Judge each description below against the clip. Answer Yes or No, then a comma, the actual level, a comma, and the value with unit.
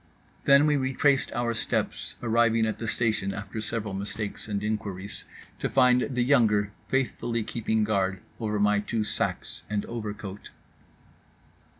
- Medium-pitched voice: No, low, 110 Hz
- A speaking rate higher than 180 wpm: No, slow, 135 wpm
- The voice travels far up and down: No, narrow, 2.6 semitones